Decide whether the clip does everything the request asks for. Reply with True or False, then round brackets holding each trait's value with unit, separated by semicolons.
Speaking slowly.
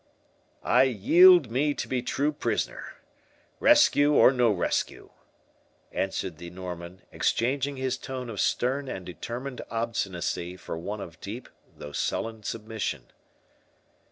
True (125 wpm)